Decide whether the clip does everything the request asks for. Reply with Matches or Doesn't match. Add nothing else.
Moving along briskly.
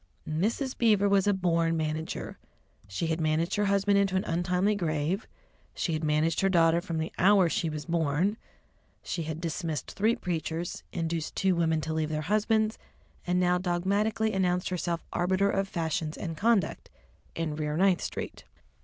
Doesn't match